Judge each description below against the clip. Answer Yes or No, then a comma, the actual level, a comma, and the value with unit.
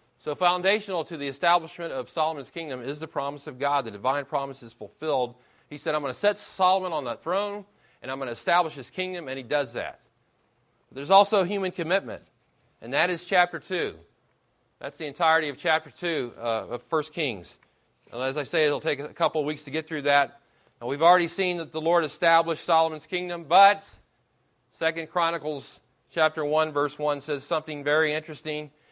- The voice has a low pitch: No, medium, 155 Hz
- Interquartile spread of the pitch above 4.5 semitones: No, average, 3.5 semitones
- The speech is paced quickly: No, average, 195 wpm